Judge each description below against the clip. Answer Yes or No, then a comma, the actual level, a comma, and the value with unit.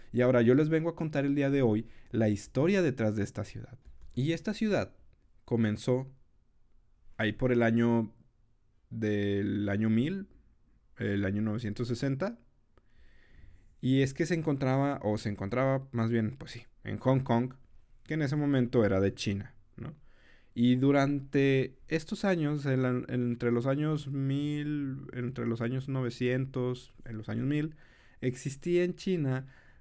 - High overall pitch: No, low, 125 Hz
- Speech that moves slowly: No, average, 150 wpm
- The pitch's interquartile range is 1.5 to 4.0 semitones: Yes, average, 3.7 semitones